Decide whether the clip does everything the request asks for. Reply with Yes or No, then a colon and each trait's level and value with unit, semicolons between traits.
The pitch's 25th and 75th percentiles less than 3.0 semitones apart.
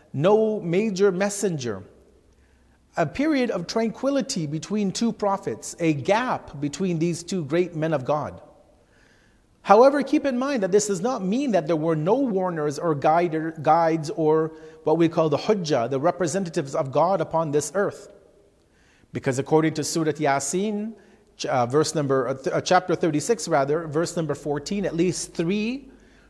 No: average, 4.8 semitones